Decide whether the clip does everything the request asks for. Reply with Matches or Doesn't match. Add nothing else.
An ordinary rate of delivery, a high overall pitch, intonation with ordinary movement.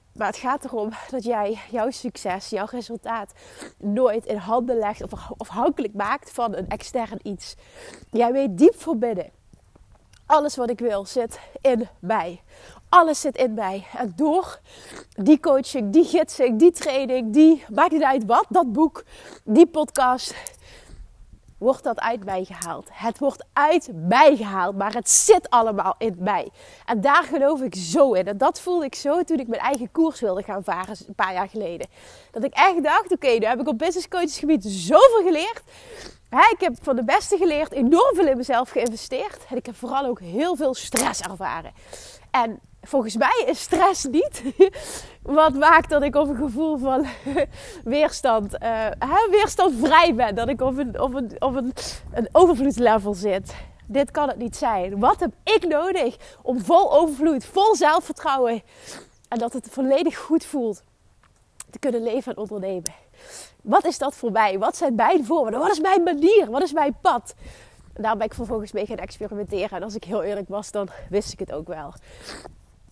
Doesn't match